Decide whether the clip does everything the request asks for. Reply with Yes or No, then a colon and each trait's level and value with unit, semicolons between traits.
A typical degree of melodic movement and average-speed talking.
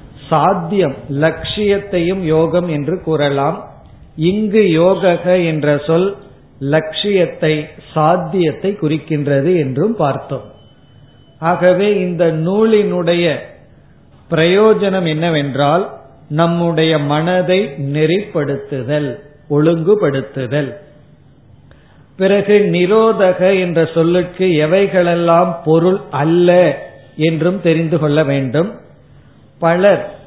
No: average, 3.7 semitones; slow, 70 wpm